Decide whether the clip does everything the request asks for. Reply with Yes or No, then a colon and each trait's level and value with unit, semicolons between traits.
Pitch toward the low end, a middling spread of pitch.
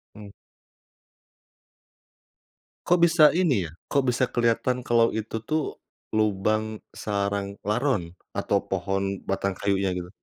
Yes: low, 110 Hz; average, 3.9 semitones